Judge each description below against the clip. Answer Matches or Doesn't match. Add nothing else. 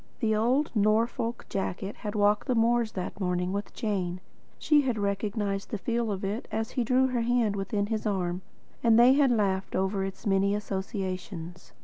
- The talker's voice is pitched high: Matches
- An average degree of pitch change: Matches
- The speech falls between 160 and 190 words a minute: Matches